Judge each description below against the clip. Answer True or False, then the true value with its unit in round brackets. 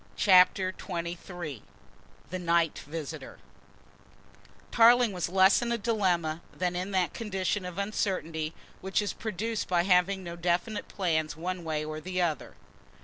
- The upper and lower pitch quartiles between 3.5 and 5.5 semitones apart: False (2.8 semitones)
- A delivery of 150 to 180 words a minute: False (140 wpm)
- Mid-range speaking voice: True (180 Hz)